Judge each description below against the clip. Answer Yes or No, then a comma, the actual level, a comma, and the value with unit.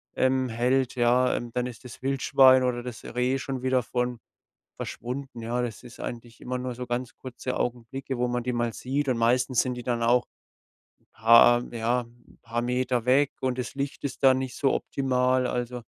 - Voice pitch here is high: No, low, 125 Hz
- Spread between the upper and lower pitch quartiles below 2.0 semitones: Yes, narrow, 1.3 semitones